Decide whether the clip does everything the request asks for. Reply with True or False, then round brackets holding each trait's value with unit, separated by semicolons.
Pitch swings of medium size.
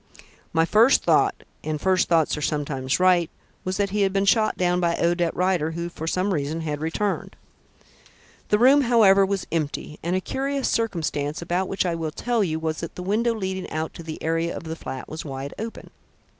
True (3.7 semitones)